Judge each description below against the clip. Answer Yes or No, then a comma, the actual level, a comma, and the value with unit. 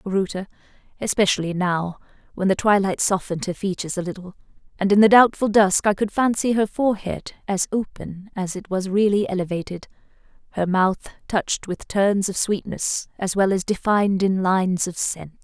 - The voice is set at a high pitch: Yes, high, 195 Hz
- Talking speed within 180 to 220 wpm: No, average, 165 wpm